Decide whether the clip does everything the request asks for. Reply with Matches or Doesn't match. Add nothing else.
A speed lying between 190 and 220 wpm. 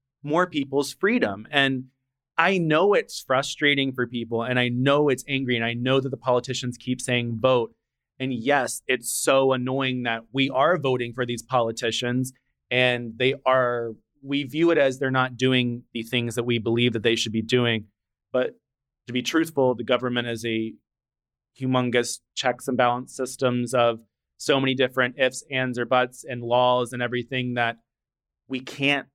Doesn't match